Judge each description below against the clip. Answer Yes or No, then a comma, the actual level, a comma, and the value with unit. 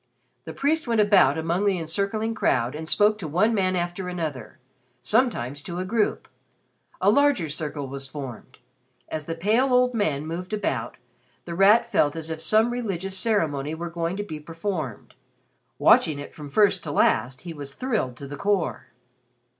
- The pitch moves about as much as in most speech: No, wide, 5.8 semitones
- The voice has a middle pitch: Yes, medium, 175 Hz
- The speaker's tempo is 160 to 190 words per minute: Yes, average, 170 wpm